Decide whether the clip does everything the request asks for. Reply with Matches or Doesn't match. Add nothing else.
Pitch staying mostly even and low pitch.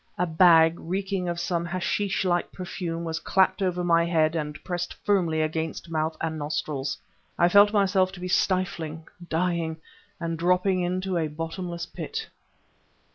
Doesn't match